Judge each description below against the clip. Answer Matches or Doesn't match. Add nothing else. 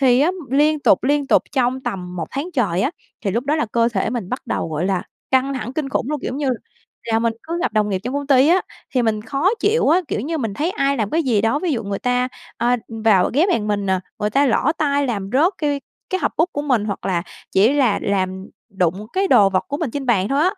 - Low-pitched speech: Doesn't match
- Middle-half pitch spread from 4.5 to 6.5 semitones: Matches